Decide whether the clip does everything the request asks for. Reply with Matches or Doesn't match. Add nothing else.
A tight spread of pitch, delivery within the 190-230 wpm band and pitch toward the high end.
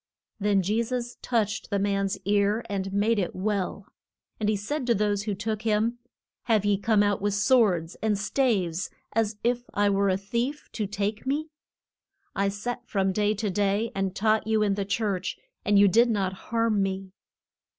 Doesn't match